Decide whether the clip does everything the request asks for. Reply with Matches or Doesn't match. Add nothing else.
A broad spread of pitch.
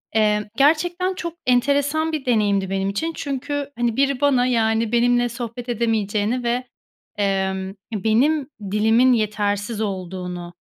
Doesn't match